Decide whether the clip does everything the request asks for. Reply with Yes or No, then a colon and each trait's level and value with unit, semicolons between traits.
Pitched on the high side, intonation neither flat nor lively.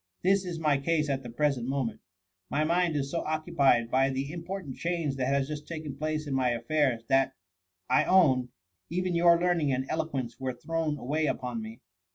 No: medium, 145 Hz; average, 3.8 semitones